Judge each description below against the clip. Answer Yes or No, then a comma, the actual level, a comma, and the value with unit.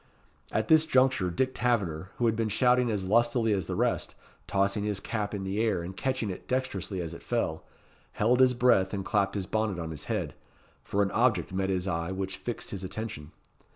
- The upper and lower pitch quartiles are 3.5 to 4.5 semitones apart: Yes, average, 4.0 semitones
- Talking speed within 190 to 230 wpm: Yes, fast, 205 wpm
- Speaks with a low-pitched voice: Yes, low, 100 Hz